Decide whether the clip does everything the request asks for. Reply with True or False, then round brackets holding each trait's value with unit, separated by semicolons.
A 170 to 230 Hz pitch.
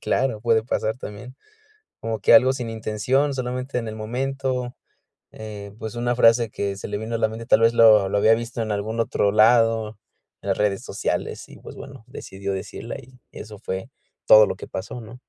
False (115 Hz)